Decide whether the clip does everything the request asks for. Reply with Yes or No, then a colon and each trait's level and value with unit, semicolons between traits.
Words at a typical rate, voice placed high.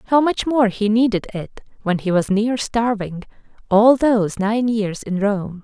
Yes: average, 180 wpm; high, 215 Hz